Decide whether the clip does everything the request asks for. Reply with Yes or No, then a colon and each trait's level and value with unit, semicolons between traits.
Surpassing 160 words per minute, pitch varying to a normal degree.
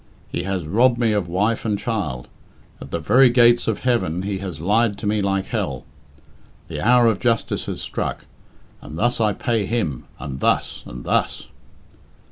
Yes: average, 175 wpm; average, 4.7 semitones